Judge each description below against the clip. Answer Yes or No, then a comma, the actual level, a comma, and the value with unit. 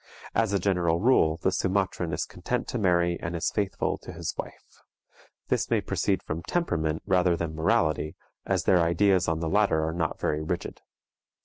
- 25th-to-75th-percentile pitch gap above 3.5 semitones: No, average, 3.2 semitones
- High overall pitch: No, very low, 85 Hz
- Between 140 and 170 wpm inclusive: No, average, 180 wpm